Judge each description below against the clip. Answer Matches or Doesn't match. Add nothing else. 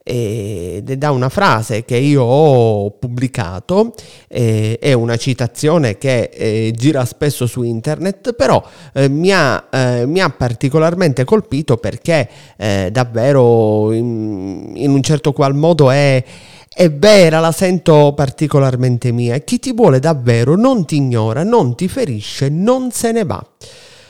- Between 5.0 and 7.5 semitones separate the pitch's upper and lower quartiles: Matches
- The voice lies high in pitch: Doesn't match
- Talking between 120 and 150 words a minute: Matches